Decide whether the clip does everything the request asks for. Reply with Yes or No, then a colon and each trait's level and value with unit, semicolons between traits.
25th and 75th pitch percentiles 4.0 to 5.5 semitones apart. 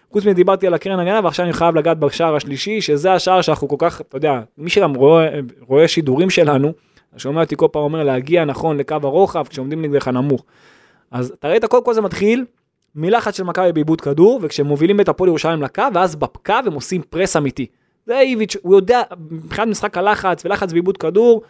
Yes: average, 5.0 semitones